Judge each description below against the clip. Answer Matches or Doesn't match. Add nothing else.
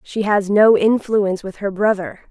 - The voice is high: Matches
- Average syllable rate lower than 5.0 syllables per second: Matches